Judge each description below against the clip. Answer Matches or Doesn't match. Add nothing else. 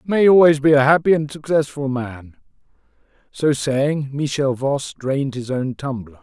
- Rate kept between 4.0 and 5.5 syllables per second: Matches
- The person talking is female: Doesn't match